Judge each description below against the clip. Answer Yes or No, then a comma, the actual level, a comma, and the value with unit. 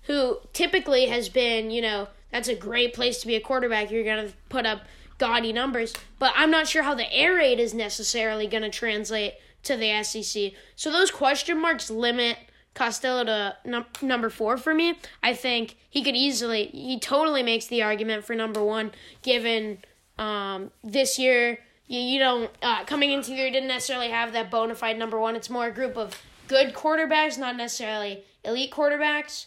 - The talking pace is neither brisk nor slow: Yes, average, 185 wpm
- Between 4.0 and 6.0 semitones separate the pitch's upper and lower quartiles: No, average, 3.2 semitones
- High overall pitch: Yes, high, 240 Hz